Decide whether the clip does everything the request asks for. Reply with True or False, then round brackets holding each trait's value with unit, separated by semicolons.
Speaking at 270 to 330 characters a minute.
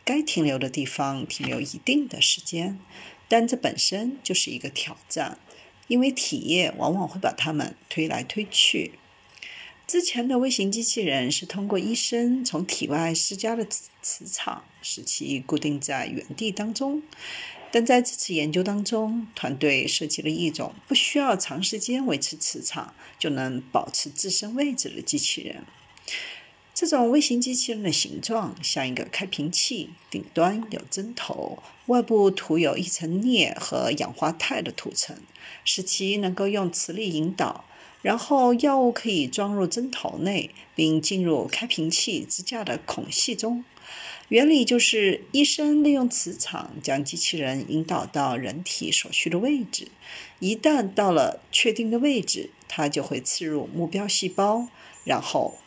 False (235 characters per minute)